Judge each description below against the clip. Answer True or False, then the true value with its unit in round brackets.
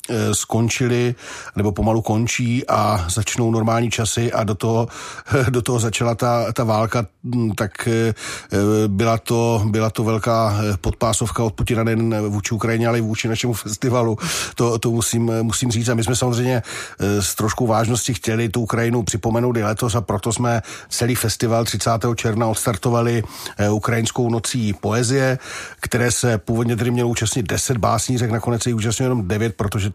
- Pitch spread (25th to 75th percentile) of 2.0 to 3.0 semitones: False (1.6 semitones)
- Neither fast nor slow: True (155 wpm)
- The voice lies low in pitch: True (115 Hz)